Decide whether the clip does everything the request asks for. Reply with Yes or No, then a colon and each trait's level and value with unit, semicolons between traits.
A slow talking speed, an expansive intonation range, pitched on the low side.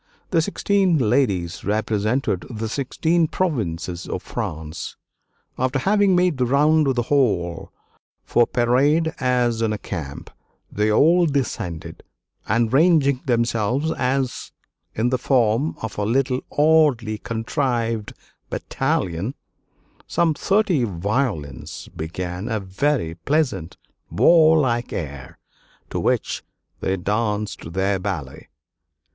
Yes: slow, 110 wpm; wide, 6.5 semitones; low, 120 Hz